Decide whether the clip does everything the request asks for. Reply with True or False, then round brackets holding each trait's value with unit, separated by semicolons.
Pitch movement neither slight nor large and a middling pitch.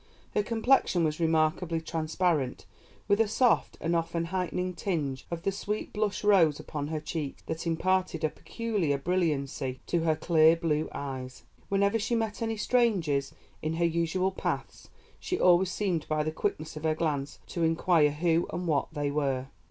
True (3.5 semitones; 165 Hz)